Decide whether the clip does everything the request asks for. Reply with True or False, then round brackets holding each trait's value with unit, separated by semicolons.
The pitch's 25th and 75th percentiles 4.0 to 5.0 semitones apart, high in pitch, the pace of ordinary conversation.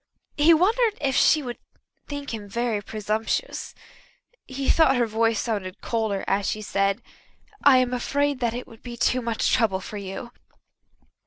True (4.3 semitones; 235 Hz; 160 wpm)